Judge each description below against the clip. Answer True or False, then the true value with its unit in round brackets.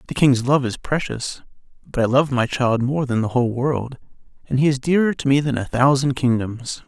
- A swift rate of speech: True (220 wpm)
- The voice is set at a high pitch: False (130 Hz)